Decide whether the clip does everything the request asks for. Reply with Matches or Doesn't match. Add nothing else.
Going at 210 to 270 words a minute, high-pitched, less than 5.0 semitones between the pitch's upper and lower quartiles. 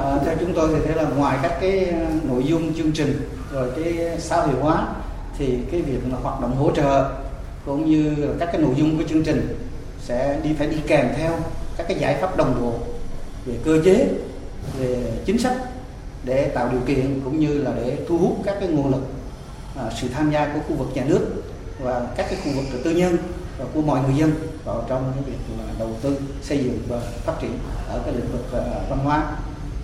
Doesn't match